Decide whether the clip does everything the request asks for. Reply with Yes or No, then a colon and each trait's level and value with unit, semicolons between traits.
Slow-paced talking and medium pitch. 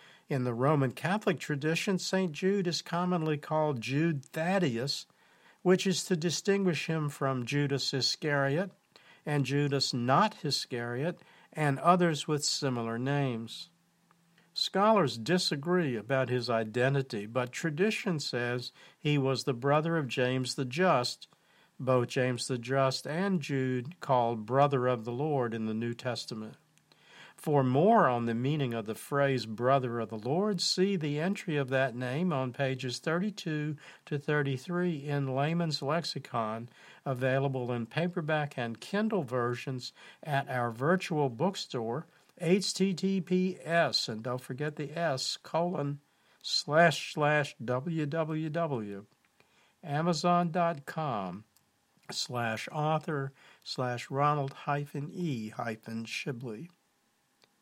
Yes: slow, 120 wpm; medium, 145 Hz